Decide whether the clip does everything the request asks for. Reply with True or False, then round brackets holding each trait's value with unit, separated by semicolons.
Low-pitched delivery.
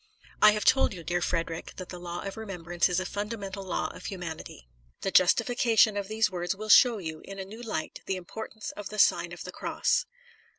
False (195 Hz)